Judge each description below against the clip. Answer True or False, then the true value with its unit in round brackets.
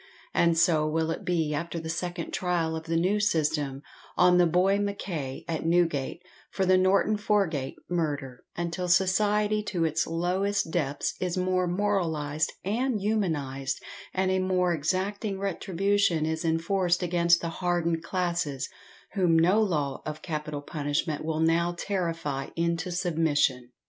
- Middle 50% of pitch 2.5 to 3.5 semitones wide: True (2.9 semitones)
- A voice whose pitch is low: False (170 Hz)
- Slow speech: False (145 wpm)